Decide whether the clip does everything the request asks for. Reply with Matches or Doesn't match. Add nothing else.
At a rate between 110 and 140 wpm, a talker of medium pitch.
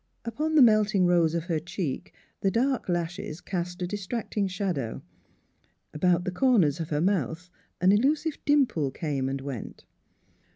Doesn't match